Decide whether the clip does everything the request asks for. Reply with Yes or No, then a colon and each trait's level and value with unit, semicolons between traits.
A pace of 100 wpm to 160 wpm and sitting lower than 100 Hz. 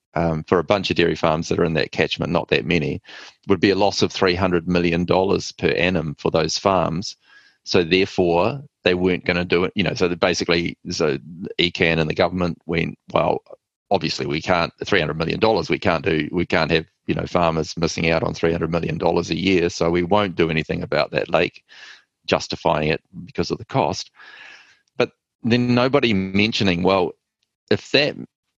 No: average, 185 wpm; very low, 90 Hz